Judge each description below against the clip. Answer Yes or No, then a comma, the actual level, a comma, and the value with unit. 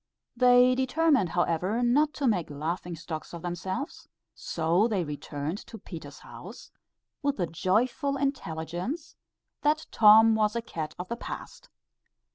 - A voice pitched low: No, high, 210 Hz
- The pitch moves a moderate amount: No, wide, 7.1 semitones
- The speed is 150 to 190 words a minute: No, slow, 135 wpm